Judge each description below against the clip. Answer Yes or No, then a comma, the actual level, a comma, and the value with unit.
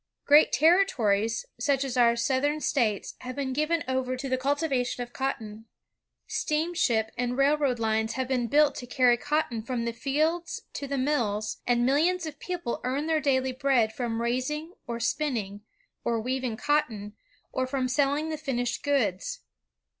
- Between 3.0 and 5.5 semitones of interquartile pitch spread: Yes, average, 3.7 semitones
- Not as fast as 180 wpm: Yes, average, 165 wpm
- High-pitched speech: Yes, very high, 260 Hz